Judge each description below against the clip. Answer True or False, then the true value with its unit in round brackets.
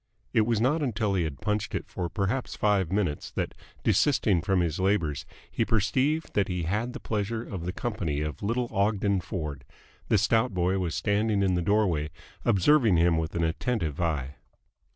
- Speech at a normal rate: True (180 wpm)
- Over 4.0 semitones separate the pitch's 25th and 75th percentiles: True (4.4 semitones)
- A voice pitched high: False (100 Hz)